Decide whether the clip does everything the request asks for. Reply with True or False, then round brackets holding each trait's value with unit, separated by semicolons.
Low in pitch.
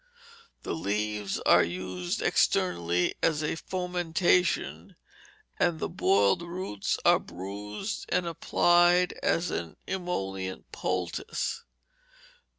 True (105 Hz)